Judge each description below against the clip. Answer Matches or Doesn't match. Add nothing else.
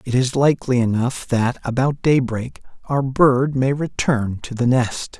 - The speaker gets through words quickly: Doesn't match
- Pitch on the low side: Matches